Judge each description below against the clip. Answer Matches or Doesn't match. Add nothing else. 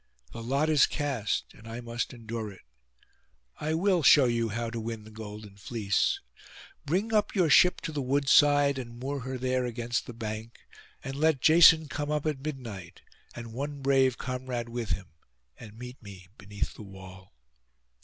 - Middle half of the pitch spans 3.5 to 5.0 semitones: Matches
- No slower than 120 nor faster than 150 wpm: Doesn't match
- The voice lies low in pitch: Matches